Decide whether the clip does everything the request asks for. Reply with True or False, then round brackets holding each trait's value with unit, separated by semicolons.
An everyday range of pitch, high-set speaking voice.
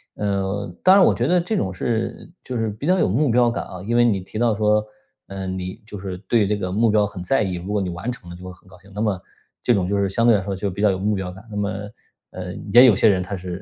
False (3.5 semitones; 100 Hz)